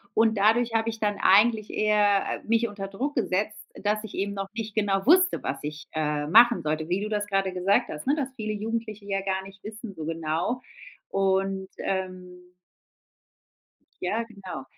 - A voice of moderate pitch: No, high, 200 Hz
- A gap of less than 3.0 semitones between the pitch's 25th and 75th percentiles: Yes, narrow, 2.6 semitones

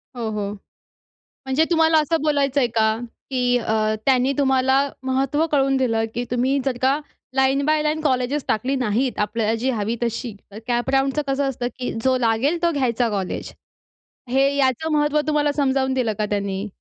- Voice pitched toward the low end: No, very high, 260 Hz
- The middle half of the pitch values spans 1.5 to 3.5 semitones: Yes, average, 3.1 semitones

